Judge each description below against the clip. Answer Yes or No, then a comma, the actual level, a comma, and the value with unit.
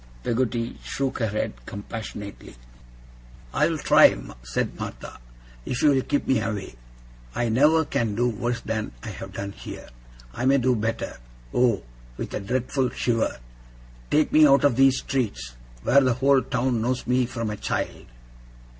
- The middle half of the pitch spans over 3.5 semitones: No, average, 3.0 semitones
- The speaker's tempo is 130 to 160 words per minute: Yes, average, 155 wpm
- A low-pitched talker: Yes, low, 120 Hz